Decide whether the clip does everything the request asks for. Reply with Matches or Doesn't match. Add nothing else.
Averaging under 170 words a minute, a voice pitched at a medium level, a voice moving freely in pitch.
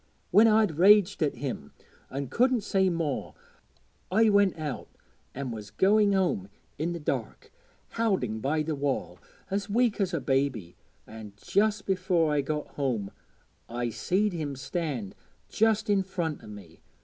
Matches